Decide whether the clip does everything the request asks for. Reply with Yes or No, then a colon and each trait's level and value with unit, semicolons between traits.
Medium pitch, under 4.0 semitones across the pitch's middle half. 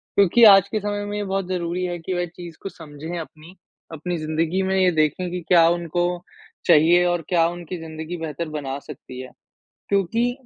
Yes: medium, 175 Hz; average, 2.7 semitones